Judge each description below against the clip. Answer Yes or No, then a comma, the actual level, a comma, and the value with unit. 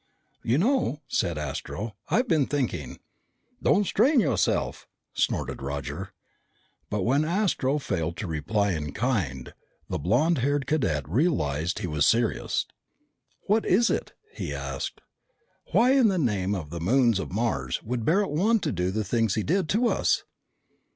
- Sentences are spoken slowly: No, average, 150 wpm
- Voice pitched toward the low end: Yes, low, 115 Hz